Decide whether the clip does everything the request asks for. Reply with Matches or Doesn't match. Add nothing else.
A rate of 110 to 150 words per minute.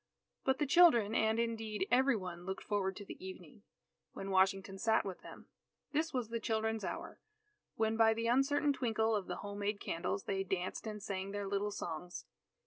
Doesn't match